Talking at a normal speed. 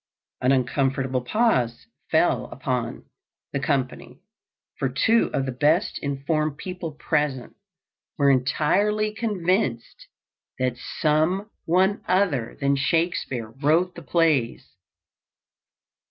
No: slow, 100 wpm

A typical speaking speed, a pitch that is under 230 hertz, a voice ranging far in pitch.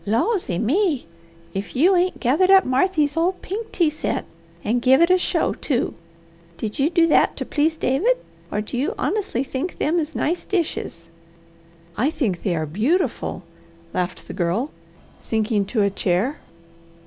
No: average, 160 wpm; very high, 280 Hz; wide, 8.4 semitones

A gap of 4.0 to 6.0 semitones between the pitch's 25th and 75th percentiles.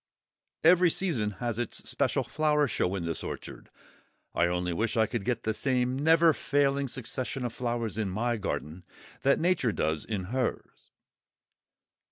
Yes: average, 5.2 semitones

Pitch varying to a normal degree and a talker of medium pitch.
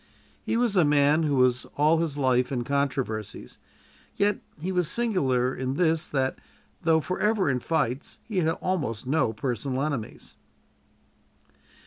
Yes: average, 4.5 semitones; medium, 145 Hz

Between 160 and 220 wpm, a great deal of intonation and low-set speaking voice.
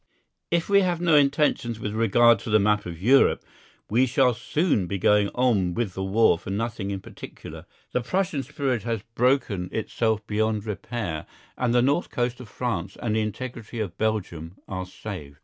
No: average, 180 wpm; average, 4.1 semitones; low, 110 Hz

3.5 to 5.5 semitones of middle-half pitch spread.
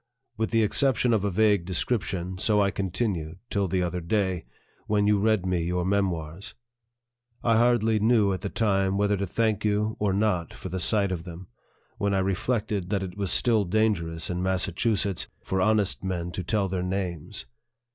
No: average, 2.9 semitones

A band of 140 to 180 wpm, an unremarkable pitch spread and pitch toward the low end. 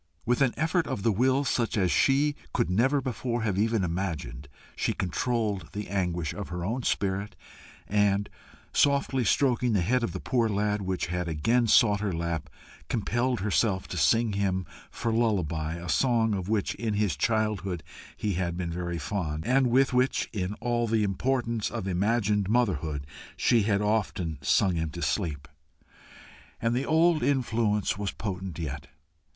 Yes: average, 165 wpm; average, 5.0 semitones; low, 105 Hz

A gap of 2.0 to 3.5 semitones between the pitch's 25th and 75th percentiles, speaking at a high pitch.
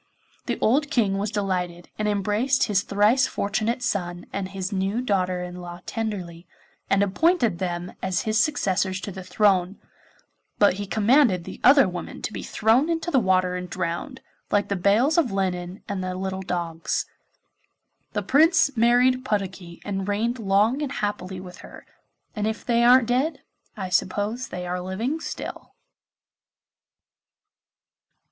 No: average, 4.4 semitones; high, 200 Hz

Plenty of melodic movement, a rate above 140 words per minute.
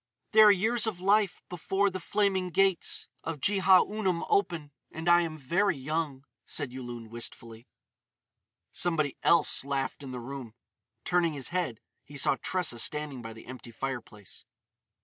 Yes: wide, 6.2 semitones; average, 150 wpm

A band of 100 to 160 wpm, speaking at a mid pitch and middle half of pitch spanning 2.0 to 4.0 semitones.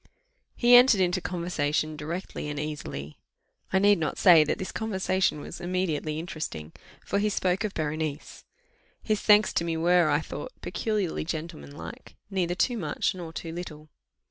Yes: average, 155 wpm; medium, 170 Hz; average, 3.7 semitones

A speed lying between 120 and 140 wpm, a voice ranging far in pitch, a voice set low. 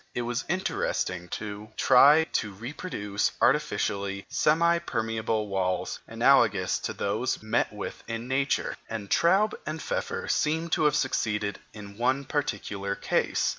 Yes: slow, 135 wpm; wide, 6.6 semitones; low, 115 Hz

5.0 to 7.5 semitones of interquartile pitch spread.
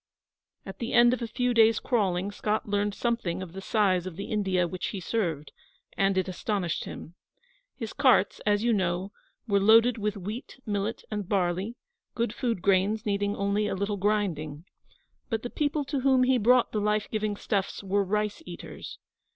No: average, 3.1 semitones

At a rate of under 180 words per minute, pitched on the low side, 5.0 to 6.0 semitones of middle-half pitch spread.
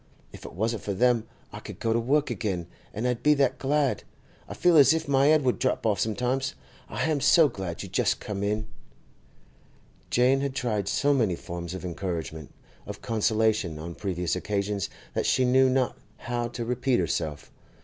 No: average, 185 wpm; low, 115 Hz; average, 5.3 semitones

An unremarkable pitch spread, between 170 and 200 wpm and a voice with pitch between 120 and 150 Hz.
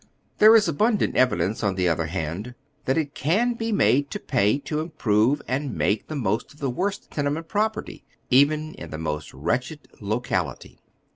No: wide, 7.7 semitones; average, 180 wpm; low, 135 Hz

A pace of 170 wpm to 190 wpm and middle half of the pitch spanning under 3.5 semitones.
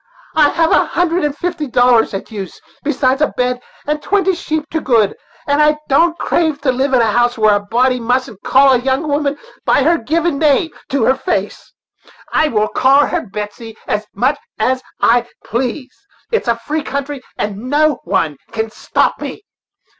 No: average, 185 wpm; average, 4.5 semitones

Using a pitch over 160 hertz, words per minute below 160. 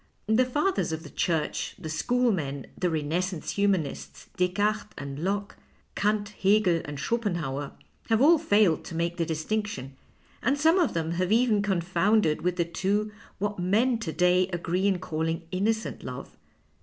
No: medium, 185 Hz; average, 170 wpm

